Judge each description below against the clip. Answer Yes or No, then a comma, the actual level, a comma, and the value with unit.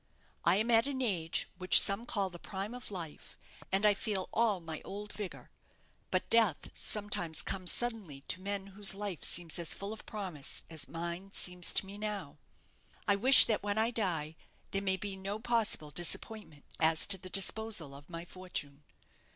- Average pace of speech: Yes, average, 180 wpm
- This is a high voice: Yes, high, 195 Hz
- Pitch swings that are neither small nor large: Yes, average, 3.6 semitones